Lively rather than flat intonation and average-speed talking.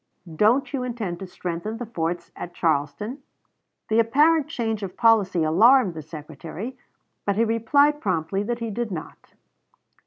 Yes: wide, 5.8 semitones; average, 150 wpm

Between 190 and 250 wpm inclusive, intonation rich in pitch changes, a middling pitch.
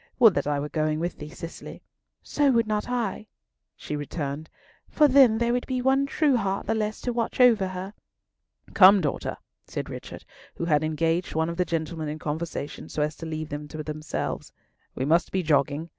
Yes: average, 195 wpm; wide, 6.5 semitones; medium, 170 Hz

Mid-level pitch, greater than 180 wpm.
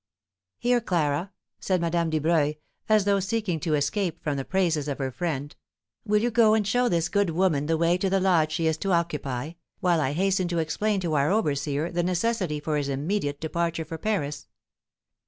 Yes: medium, 170 Hz; average, 190 wpm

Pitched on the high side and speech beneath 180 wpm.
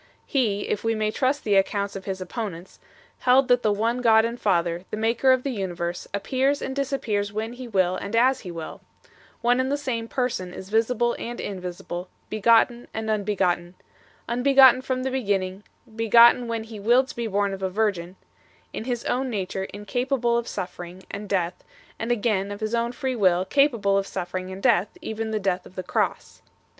No: high, 220 Hz; average, 190 wpm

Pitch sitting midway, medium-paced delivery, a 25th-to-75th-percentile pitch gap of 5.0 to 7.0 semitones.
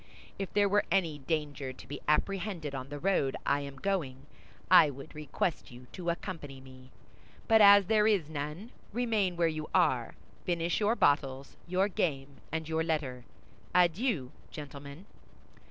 Yes: medium, 160 Hz; average, 155 wpm; average, 5.3 semitones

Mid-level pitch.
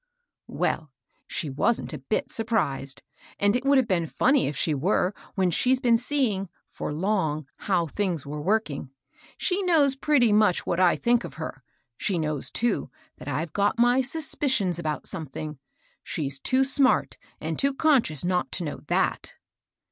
No: high, 195 Hz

